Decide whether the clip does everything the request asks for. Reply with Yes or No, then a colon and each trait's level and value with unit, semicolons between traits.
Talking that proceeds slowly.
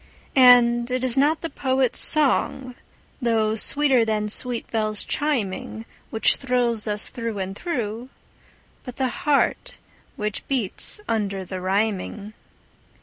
Yes: slow, 125 wpm